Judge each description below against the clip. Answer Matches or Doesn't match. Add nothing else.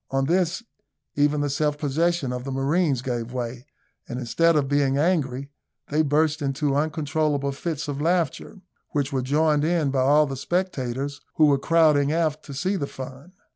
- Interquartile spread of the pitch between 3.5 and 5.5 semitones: Doesn't match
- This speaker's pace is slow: Doesn't match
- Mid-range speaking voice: Matches